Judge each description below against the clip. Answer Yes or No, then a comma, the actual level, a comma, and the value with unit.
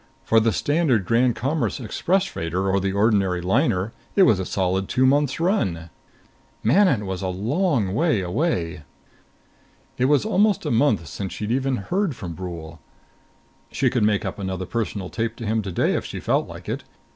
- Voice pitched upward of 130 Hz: No, low, 110 Hz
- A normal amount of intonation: No, wide, 6.6 semitones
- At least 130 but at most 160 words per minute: No, average, 175 wpm